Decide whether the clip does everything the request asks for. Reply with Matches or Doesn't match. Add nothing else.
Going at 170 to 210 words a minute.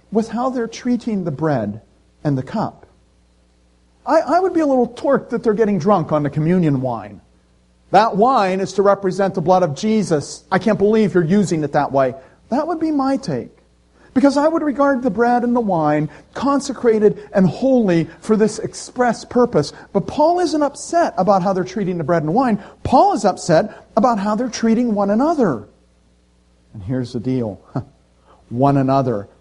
Matches